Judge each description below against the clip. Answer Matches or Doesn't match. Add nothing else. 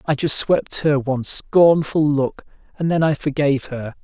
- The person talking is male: Matches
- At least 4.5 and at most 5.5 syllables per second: Matches